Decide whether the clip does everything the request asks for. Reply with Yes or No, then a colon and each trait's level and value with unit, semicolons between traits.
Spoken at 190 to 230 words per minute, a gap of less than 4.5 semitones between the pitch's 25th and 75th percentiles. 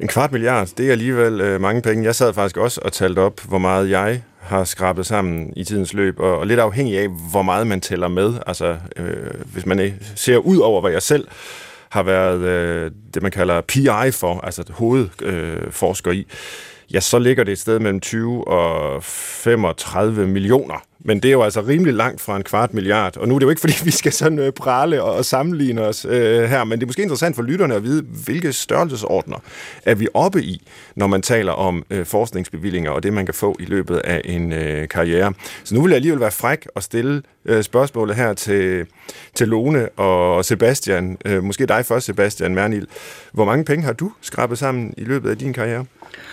No: average, 205 wpm; average, 5.0 semitones